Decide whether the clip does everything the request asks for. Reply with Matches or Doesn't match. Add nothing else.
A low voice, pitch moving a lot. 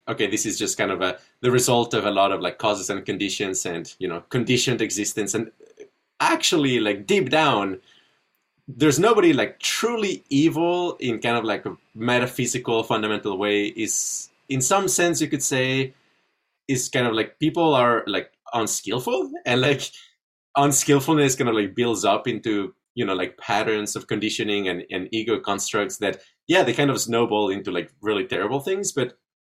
Matches